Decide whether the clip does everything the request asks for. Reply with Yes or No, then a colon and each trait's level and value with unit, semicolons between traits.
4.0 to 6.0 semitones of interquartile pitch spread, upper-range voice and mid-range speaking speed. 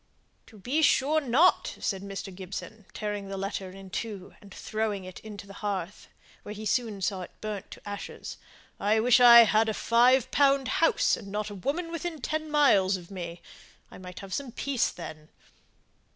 Yes: average, 4.3 semitones; high, 210 Hz; average, 180 wpm